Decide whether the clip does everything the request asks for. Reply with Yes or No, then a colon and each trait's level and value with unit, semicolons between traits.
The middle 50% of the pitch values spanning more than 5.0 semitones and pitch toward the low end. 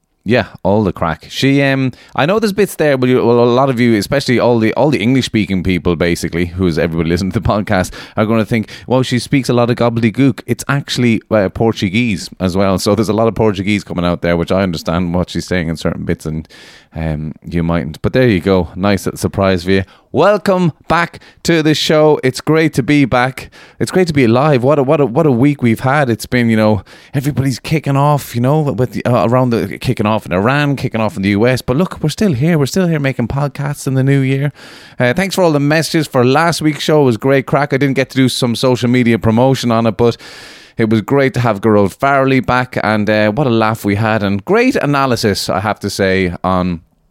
Yes: wide, 5.6 semitones; low, 120 Hz